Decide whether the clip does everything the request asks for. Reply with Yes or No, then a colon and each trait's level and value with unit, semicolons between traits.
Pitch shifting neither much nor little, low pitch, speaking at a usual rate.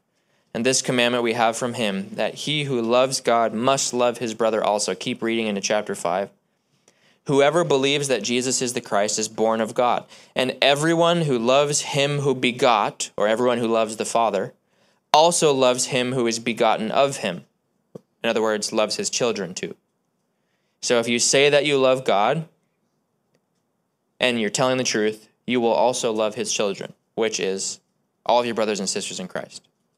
Yes: average, 3.6 semitones; low, 125 Hz; average, 180 wpm